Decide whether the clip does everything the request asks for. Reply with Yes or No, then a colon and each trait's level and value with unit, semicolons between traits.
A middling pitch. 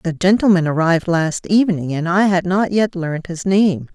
Yes: medium, 180 Hz